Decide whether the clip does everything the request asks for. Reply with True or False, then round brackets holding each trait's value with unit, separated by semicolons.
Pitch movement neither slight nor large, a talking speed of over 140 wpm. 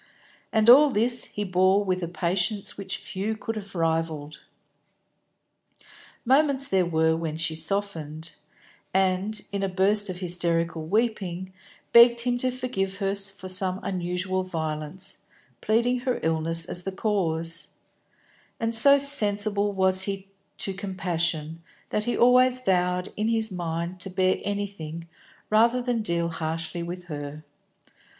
False (4.1 semitones; 135 wpm)